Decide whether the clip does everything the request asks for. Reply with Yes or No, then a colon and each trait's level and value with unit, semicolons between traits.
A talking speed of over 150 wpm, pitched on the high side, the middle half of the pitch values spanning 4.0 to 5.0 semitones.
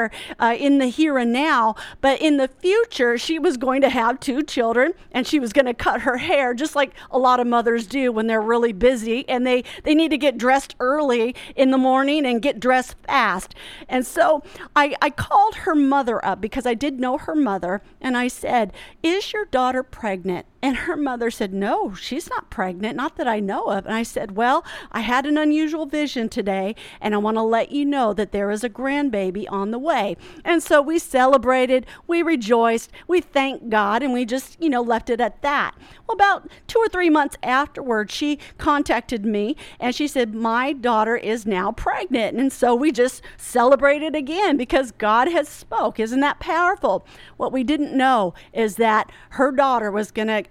Yes: average, 200 wpm; very high, 255 Hz; average, 4.4 semitones